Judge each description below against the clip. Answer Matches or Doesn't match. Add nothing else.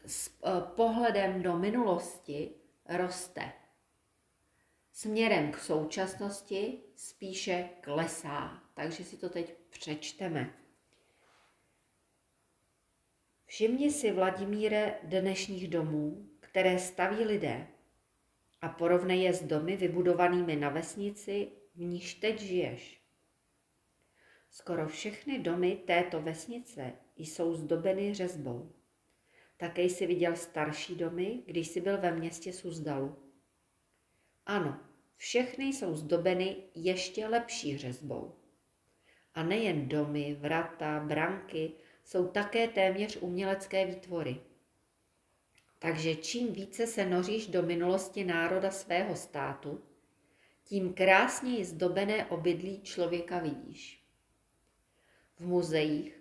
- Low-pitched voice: Doesn't match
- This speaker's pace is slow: Matches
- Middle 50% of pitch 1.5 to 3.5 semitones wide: Matches